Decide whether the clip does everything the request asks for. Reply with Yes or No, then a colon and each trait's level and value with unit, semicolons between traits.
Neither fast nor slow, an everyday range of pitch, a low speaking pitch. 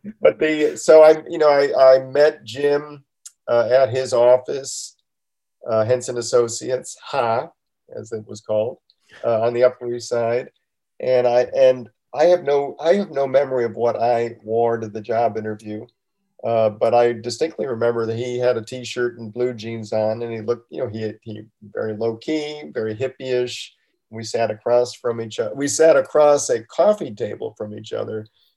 Yes: average, 185 wpm; average, 3.3 semitones; low, 120 Hz